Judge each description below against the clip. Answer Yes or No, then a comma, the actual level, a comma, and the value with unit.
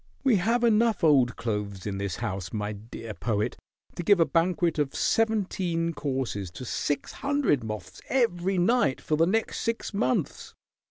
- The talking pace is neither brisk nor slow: Yes, average, 160 wpm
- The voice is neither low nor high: Yes, medium, 160 Hz